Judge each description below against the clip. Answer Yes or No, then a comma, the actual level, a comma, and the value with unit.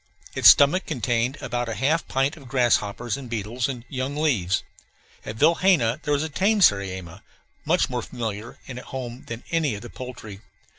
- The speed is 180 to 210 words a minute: Yes, average, 185 wpm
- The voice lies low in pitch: Yes, low, 125 Hz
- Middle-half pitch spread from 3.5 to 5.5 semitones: Yes, average, 4.0 semitones